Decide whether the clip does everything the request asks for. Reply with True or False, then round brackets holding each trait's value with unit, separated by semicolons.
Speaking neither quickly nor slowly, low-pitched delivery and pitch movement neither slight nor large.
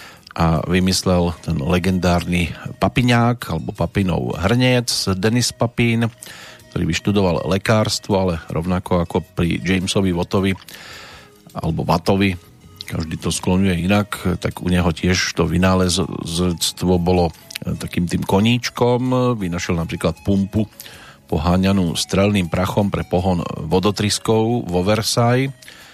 False (105 wpm; 95 Hz; 3.4 semitones)